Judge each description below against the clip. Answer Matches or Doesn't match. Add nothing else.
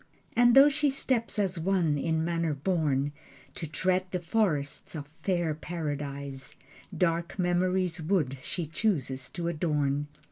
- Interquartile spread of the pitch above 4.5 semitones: Doesn't match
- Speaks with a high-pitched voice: Doesn't match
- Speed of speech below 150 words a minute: Matches